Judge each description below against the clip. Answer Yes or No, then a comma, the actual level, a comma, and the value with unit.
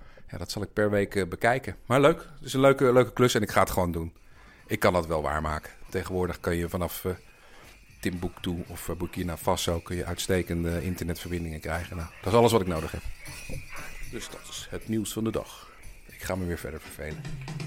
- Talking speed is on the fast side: Yes, fast, 210 wpm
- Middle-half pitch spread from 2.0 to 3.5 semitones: No, average, 4.4 semitones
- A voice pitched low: Yes, very low, 90 Hz